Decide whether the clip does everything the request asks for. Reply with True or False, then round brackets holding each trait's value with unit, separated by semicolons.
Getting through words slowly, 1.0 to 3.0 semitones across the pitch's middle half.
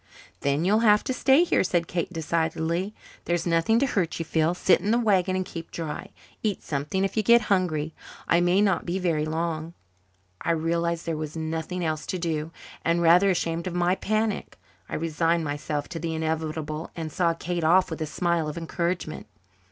False (195 wpm; 2.5 semitones)